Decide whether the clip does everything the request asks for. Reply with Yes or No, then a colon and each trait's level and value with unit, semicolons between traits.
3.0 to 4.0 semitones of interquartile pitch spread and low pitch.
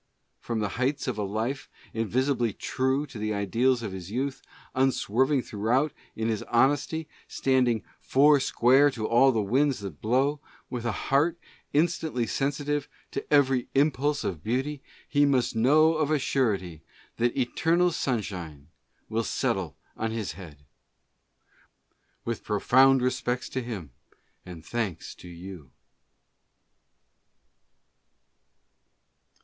No: average, 4.4 semitones; low, 125 Hz